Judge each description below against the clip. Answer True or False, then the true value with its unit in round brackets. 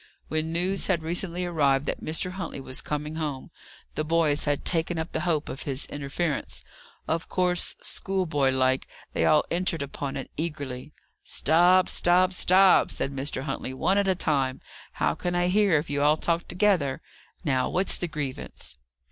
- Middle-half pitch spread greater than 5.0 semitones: False (3.9 semitones)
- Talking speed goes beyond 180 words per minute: False (170 wpm)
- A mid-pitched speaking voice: True (160 Hz)